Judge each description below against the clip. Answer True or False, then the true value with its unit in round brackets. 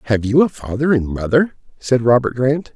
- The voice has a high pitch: False (130 Hz)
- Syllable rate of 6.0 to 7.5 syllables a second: False (5.2 syllables/s)